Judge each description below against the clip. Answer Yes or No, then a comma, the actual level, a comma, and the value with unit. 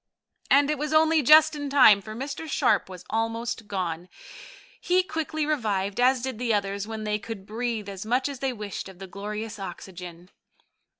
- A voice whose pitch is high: Yes, high, 225 Hz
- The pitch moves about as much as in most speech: No, wide, 5.9 semitones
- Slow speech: No, average, 180 wpm